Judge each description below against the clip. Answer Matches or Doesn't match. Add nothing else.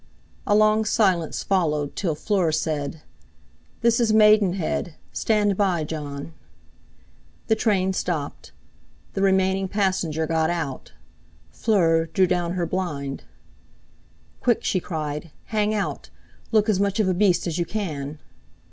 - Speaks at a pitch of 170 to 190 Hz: Matches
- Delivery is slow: Matches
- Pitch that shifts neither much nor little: Matches